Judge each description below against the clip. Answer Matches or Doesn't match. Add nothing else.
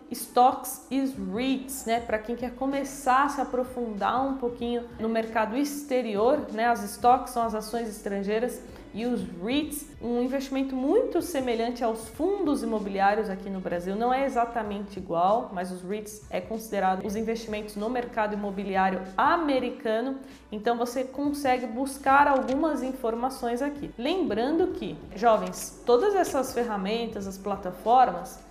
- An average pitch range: Matches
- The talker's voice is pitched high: Matches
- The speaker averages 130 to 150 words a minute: Matches